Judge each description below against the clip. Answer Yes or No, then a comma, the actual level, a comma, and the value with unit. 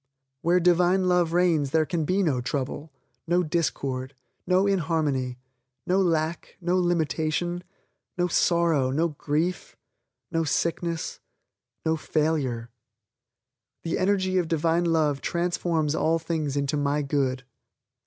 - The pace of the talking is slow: Yes, slow, 120 wpm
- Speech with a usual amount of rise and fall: Yes, average, 3.0 semitones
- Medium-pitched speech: Yes, medium, 165 Hz